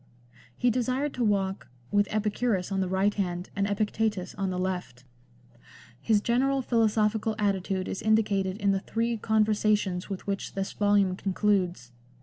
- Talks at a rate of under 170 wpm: Yes, average, 155 wpm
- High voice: Yes, high, 205 Hz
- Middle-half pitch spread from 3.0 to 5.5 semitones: No, narrow, 2.4 semitones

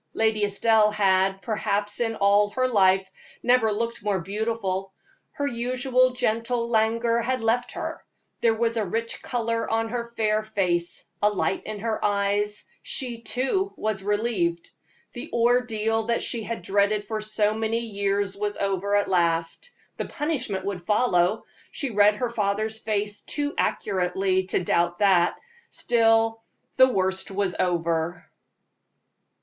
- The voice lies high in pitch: Yes, high, 215 Hz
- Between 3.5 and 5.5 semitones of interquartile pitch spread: No, average, 2.9 semitones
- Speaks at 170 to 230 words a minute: No, average, 140 wpm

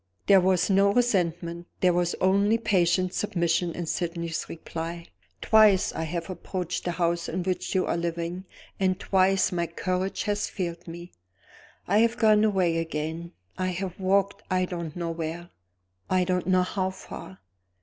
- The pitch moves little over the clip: Yes, narrow, 2.0 semitones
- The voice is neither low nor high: Yes, medium, 180 Hz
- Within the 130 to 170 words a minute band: Yes, average, 160 wpm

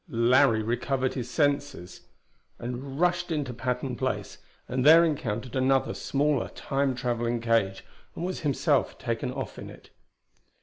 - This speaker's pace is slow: Yes, slow, 130 wpm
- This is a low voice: Yes, low, 130 Hz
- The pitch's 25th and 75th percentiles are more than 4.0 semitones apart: No, average, 3.2 semitones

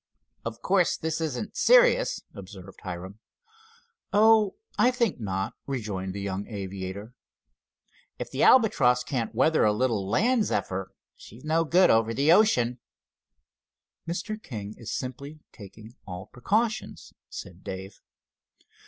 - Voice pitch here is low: Yes, low, 120 Hz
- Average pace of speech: No, slow, 125 wpm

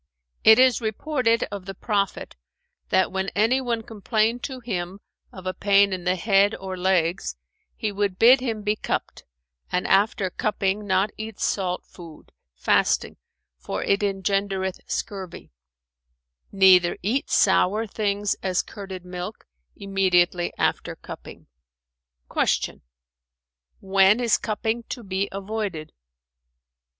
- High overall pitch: Yes, high, 195 Hz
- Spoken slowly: Yes, slow, 120 wpm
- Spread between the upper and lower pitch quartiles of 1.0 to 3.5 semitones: Yes, narrow, 2.6 semitones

